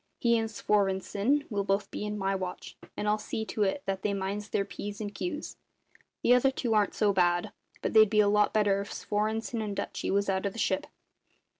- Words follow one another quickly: Yes, fast, 215 wpm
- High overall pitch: Yes, high, 205 Hz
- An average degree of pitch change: No, narrow, 1.8 semitones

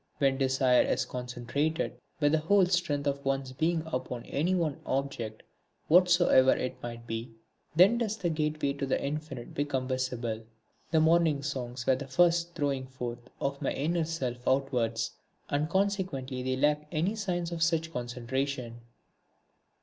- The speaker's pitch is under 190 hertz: Yes, medium, 140 Hz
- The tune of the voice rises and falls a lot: No, average, 4.3 semitones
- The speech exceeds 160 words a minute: No, average, 150 wpm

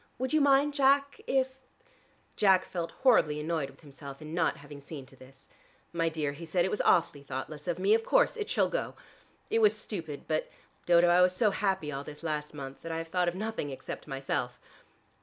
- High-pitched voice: No, medium, 165 Hz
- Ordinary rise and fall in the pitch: No, wide, 6.3 semitones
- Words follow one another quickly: Yes, fast, 215 wpm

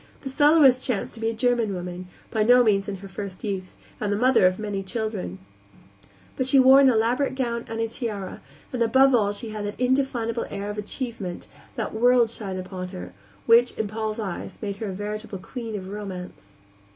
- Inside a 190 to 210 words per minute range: Yes, average, 200 wpm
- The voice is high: Yes, high, 220 Hz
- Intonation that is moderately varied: Yes, average, 3.7 semitones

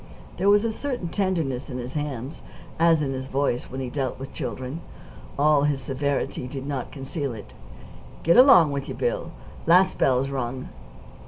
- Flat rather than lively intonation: No, average, 4.1 semitones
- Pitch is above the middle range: No, medium, 140 Hz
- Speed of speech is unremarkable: Yes, average, 170 wpm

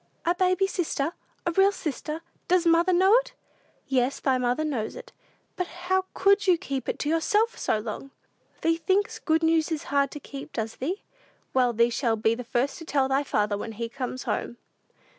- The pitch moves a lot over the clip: Yes, wide, 6.1 semitones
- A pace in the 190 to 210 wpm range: Yes, average, 195 wpm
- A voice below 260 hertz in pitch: No, very high, 305 Hz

